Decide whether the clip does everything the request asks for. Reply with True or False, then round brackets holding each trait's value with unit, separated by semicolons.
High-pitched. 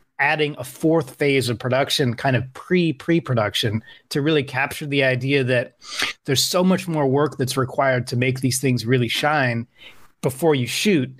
False (135 Hz)